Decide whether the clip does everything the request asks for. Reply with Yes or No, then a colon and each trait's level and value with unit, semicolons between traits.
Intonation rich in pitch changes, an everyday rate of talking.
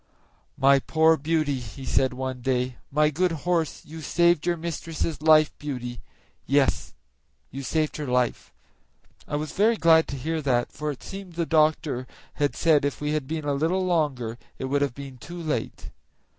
No: average, 3.3 semitones; average, 175 wpm